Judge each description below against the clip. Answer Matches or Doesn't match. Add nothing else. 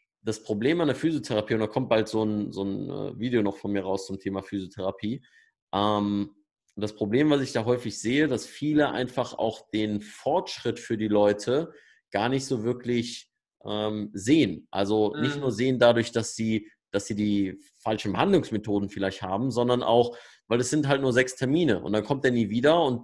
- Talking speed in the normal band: Doesn't match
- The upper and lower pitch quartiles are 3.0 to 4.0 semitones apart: Matches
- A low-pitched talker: Matches